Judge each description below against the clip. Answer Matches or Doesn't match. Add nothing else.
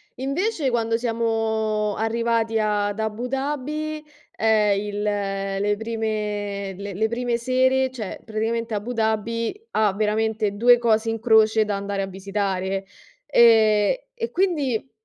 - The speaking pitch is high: Matches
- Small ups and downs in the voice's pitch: Matches